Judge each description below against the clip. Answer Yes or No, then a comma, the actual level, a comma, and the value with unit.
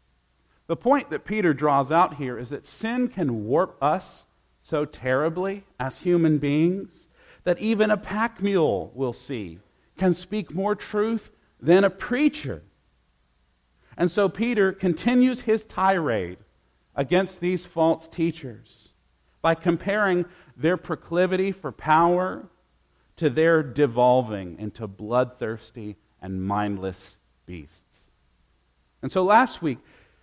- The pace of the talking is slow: Yes, slow, 120 wpm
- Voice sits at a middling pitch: Yes, medium, 155 Hz